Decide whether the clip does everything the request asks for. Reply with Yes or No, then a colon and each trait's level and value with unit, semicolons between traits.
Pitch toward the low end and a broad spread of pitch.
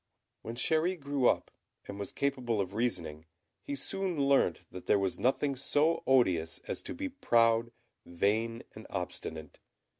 Yes: low, 120 Hz; wide, 6.4 semitones